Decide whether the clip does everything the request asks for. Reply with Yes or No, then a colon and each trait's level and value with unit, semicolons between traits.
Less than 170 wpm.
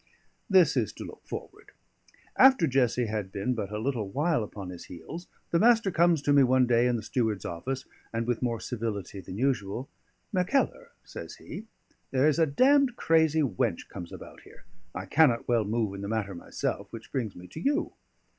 No: average, 190 wpm